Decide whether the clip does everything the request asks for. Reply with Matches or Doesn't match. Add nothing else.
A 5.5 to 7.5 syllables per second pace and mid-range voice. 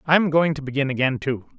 Matches